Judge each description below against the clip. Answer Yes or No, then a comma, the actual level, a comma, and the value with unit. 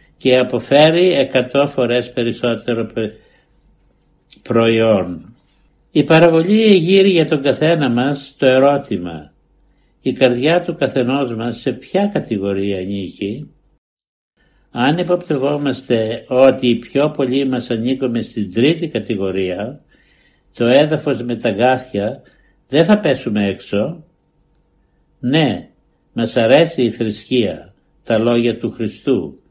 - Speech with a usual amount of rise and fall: Yes, average, 4.1 semitones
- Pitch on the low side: Yes, low, 125 Hz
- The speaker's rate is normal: No, slow, 110 wpm